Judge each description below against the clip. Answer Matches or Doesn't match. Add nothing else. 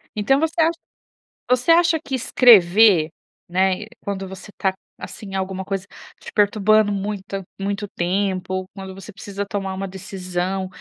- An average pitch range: Doesn't match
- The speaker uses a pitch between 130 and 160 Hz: Doesn't match